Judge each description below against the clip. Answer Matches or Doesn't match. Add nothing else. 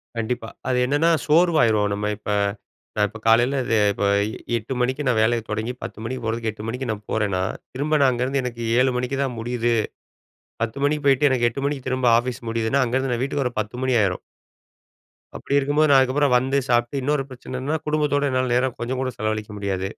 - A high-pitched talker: Doesn't match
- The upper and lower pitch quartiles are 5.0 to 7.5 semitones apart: Doesn't match